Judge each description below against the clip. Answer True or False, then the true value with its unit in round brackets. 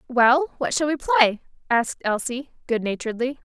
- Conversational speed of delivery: True (155 wpm)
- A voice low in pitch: False (250 Hz)